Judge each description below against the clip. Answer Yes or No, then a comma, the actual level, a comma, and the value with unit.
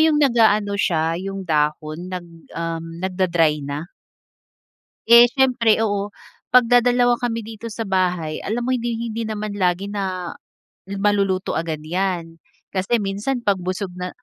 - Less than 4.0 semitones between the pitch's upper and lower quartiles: No, average, 4.6 semitones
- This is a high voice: Yes, high, 195 Hz